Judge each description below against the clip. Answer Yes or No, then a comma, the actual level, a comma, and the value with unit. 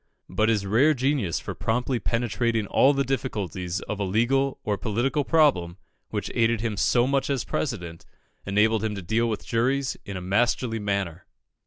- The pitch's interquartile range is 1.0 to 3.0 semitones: No, average, 4.5 semitones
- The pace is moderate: Yes, average, 170 wpm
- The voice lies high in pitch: No, low, 115 Hz